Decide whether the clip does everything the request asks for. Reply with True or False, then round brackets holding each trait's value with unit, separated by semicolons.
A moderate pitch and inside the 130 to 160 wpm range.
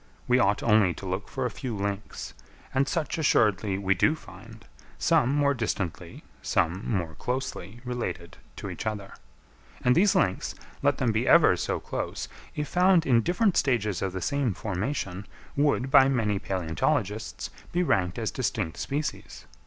False (110 Hz; 155 wpm)